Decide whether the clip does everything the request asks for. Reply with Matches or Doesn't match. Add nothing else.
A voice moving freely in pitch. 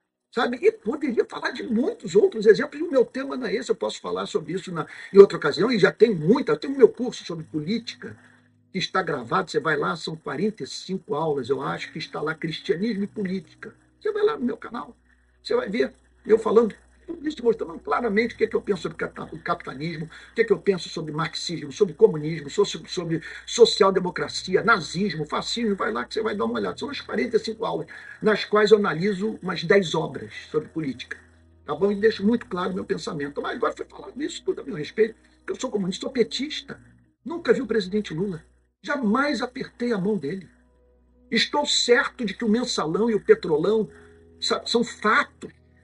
Matches